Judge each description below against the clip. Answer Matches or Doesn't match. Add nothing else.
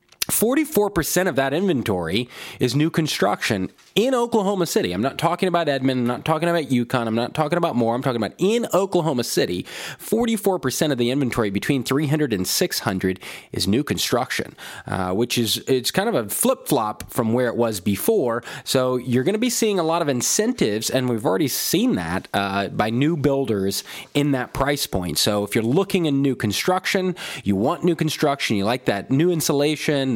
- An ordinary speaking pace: Matches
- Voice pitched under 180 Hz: Matches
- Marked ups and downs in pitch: Matches